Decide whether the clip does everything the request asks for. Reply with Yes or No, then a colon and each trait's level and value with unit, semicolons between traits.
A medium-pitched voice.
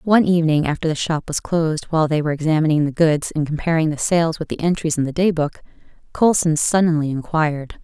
Yes: medium, 160 Hz